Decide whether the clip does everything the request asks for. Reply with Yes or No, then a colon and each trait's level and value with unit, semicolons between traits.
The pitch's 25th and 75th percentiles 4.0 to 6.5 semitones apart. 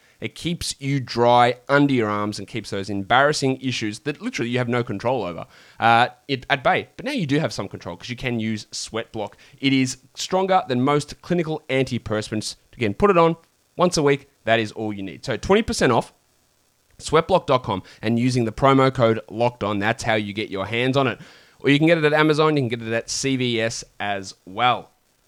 Yes: average, 4.4 semitones